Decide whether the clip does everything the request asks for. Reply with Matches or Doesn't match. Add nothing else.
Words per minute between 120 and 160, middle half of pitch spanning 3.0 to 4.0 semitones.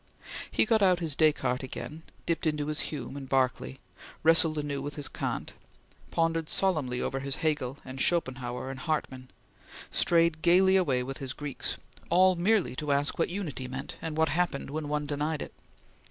Doesn't match